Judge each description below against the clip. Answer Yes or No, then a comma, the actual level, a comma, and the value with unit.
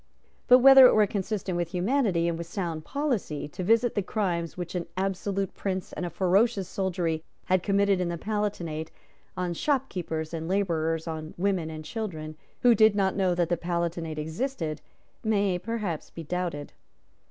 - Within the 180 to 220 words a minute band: No, average, 165 wpm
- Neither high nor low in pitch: Yes, medium, 180 Hz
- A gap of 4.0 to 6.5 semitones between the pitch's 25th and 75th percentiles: No, average, 3.6 semitones